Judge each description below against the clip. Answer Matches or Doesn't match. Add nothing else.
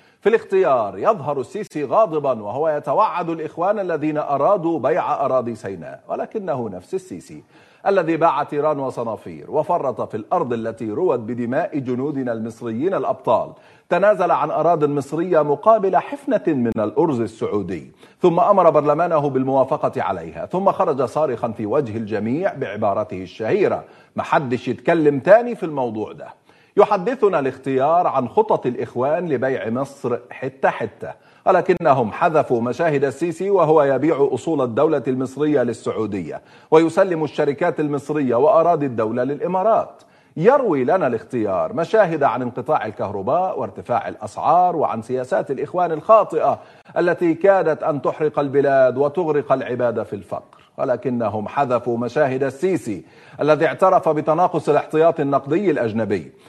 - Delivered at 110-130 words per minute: Matches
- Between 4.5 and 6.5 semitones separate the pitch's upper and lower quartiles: Matches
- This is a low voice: Doesn't match